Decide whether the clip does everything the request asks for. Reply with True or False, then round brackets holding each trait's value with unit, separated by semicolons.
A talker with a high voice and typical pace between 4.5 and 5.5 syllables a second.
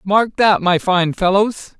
False (195 Hz; 3.6 syllables/s)